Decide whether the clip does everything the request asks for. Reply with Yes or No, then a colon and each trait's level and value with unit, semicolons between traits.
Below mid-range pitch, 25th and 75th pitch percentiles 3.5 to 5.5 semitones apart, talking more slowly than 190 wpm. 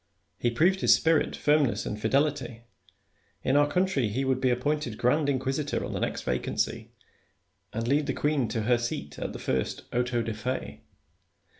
Yes: low, 130 Hz; average, 3.8 semitones; average, 170 wpm